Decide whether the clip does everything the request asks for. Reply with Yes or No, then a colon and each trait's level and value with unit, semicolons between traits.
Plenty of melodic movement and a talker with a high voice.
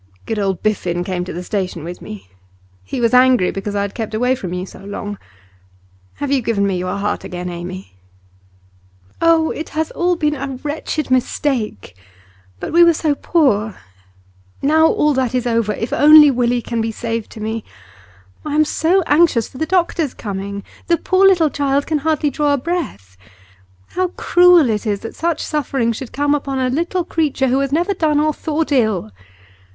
Yes: wide, 6.9 semitones; very high, 255 Hz